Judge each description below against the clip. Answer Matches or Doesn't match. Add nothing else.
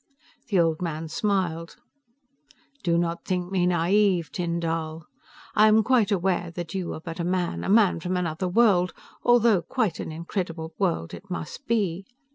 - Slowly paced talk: Doesn't match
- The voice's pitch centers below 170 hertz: Doesn't match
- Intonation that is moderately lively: Matches